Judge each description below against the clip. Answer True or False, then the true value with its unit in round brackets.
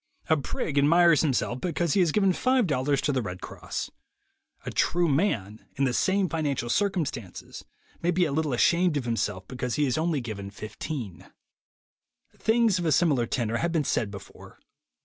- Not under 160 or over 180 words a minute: True (170 wpm)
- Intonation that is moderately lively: False (6.3 semitones)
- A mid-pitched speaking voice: True (145 Hz)